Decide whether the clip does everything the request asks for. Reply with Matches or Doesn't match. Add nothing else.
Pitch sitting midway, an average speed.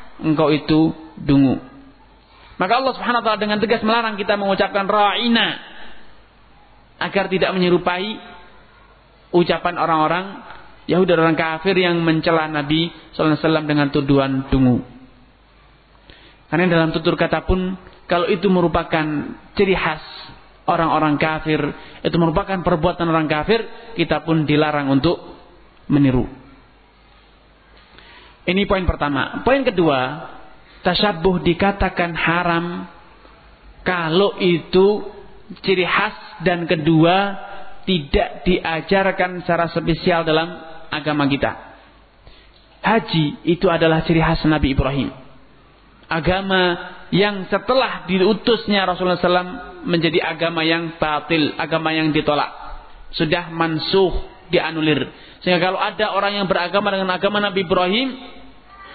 Matches